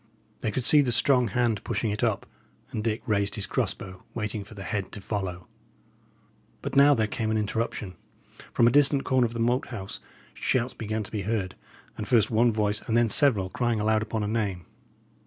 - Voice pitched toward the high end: No, low, 110 Hz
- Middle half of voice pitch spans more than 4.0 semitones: No, narrow, 2.5 semitones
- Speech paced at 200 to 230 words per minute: Yes, fast, 205 wpm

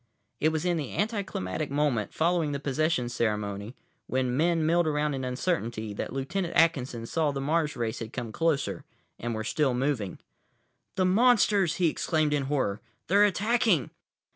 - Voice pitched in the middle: Yes, medium, 150 Hz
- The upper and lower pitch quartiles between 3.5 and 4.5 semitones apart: No, wide, 5.5 semitones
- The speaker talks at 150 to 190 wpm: Yes, average, 160 wpm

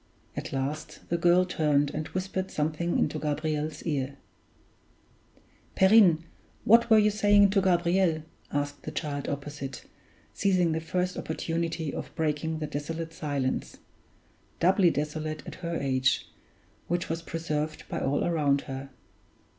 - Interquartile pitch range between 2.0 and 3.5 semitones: Yes, average, 3.1 semitones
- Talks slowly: Yes, slow, 130 wpm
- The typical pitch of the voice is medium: Yes, medium, 160 Hz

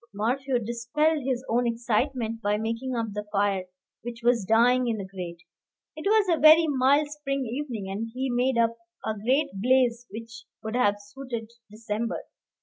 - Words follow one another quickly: No, average, 165 wpm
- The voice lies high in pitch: Yes, high, 235 Hz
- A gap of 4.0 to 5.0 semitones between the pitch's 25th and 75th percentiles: No, average, 3.2 semitones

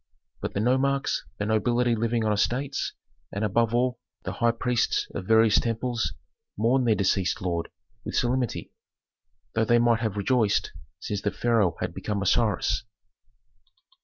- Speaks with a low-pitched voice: Yes, low, 115 Hz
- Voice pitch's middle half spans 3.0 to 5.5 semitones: No, narrow, 2.6 semitones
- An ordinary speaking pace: Yes, average, 145 wpm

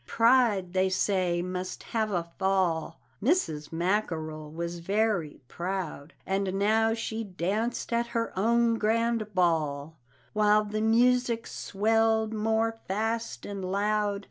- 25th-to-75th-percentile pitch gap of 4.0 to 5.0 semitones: No, average, 3.6 semitones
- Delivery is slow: Yes, slow, 125 wpm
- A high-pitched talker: Yes, high, 205 Hz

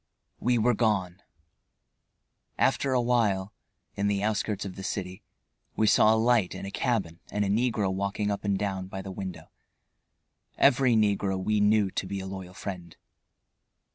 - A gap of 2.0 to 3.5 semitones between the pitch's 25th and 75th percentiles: Yes, narrow, 2.4 semitones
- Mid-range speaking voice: No, low, 100 Hz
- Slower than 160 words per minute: No, average, 165 wpm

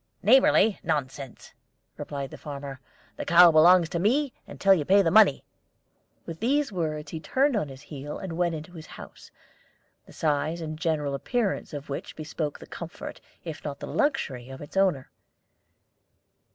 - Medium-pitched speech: Yes, medium, 160 Hz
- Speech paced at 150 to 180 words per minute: Yes, average, 165 wpm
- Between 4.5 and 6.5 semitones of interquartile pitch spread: Yes, average, 4.8 semitones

